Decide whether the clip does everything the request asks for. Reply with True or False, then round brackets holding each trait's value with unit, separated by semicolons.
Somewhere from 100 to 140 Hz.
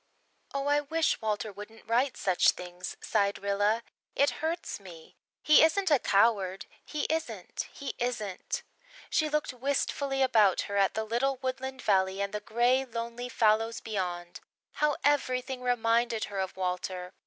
False (230 Hz)